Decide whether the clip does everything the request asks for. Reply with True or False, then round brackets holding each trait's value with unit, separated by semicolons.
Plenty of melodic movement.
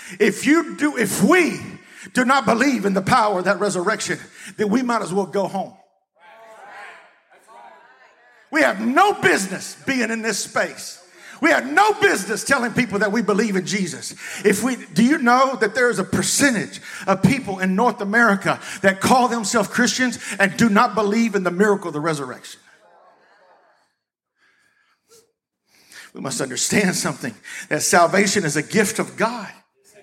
False (4.3 semitones)